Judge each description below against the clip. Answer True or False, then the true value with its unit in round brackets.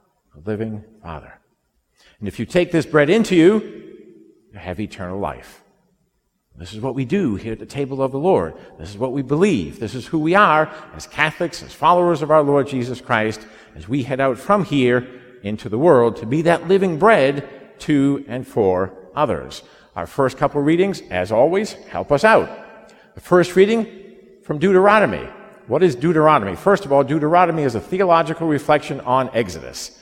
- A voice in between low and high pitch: True (145 Hz)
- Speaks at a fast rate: False (180 wpm)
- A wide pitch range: True (7.8 semitones)